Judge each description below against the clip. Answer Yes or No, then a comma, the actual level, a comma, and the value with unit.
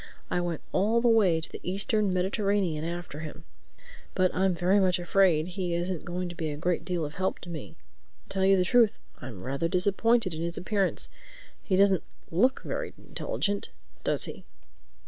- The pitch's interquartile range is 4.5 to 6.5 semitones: No, average, 2.7 semitones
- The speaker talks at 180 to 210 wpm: Yes, average, 185 wpm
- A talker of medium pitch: Yes, medium, 180 Hz